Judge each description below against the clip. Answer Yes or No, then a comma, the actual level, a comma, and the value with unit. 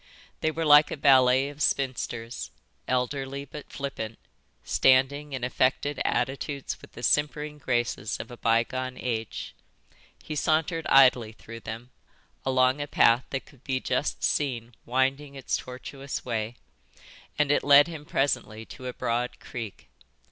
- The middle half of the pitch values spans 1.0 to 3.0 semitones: Yes, average, 2.7 semitones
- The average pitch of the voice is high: No, low, 130 Hz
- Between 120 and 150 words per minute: Yes, average, 140 wpm